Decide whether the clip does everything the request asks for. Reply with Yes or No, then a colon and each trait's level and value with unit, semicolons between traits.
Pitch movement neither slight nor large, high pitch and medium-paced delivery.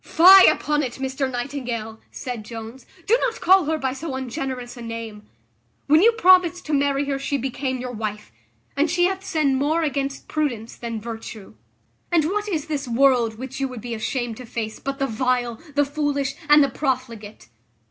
Yes: average, 4.0 semitones; very high, 265 Hz; average, 185 wpm